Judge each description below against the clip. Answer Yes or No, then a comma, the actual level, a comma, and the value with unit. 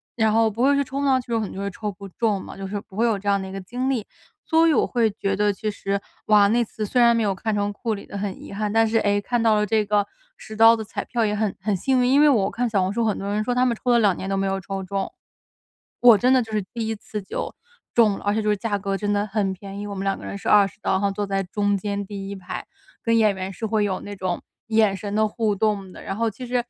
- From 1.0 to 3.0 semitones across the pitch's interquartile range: Yes, narrow, 2.4 semitones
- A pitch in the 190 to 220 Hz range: Yes, high, 210 Hz